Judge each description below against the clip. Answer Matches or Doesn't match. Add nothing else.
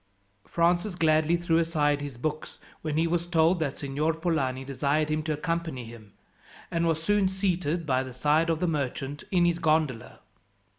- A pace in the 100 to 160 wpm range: Doesn't match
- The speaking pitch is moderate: Matches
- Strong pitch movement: Doesn't match